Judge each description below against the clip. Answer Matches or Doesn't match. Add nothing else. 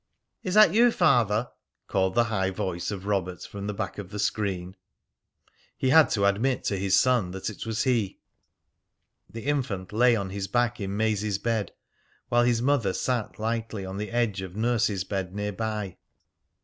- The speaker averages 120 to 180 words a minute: Matches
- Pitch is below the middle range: Matches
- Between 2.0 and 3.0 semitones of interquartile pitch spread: Doesn't match